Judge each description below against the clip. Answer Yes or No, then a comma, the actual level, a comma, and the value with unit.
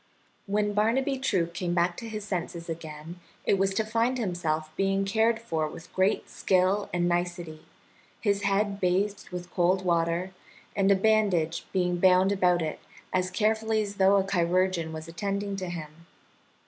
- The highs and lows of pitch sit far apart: No, average, 2.8 semitones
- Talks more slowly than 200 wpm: Yes, average, 160 wpm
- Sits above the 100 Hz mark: Yes, medium, 185 Hz